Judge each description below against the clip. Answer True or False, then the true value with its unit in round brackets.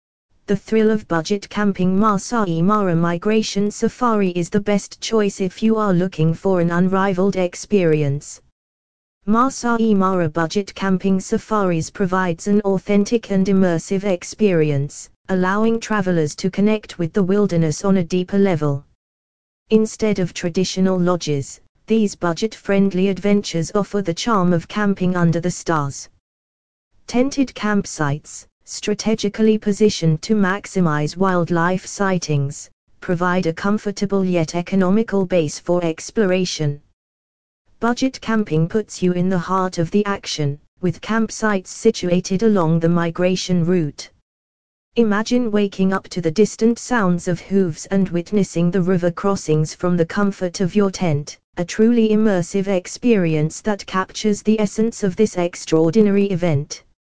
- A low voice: False (185 Hz)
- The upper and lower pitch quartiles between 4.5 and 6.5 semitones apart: False (3.8 semitones)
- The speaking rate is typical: False (130 wpm)